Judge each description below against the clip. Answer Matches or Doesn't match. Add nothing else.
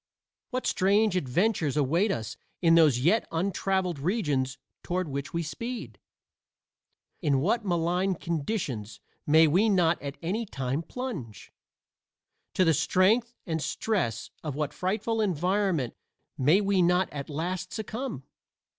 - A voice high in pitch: Doesn't match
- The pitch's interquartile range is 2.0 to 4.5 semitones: Doesn't match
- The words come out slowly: Matches